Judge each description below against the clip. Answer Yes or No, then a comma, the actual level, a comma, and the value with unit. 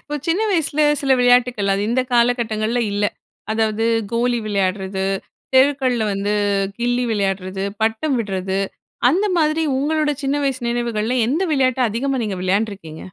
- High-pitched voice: Yes, high, 235 Hz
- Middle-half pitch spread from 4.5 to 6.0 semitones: Yes, average, 4.8 semitones